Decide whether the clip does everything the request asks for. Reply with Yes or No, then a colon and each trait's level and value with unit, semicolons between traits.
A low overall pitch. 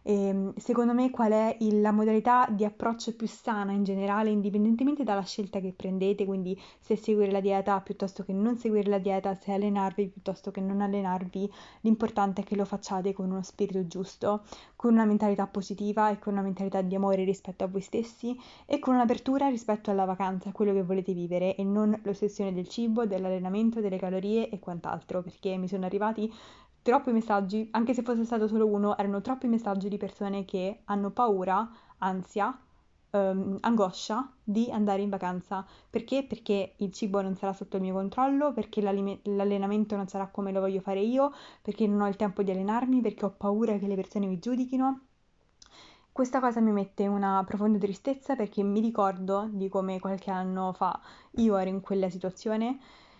No: high, 205 Hz